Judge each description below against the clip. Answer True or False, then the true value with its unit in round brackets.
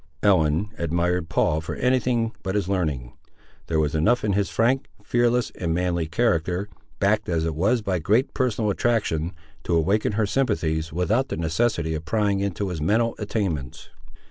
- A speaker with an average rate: True (165 wpm)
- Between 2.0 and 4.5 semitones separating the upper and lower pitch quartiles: False (5.3 semitones)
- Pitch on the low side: True (95 Hz)